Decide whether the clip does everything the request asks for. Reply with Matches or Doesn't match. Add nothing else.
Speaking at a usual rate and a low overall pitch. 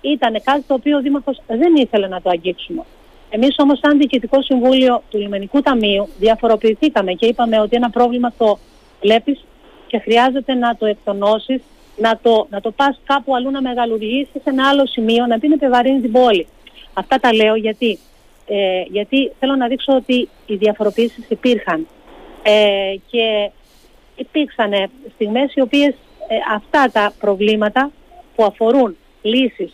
Doesn't match